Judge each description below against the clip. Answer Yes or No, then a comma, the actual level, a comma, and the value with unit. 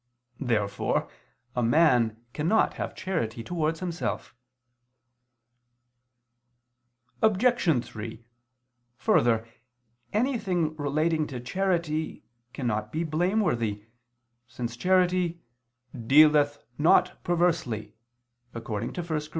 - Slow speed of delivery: Yes, slow, 75 wpm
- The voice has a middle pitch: Yes, medium, 155 Hz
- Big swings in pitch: Yes, wide, 6.9 semitones